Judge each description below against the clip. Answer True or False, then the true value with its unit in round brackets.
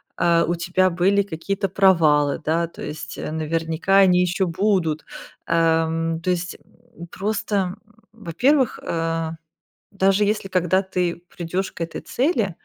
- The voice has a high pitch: False (175 Hz)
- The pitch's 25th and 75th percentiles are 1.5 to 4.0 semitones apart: True (2.9 semitones)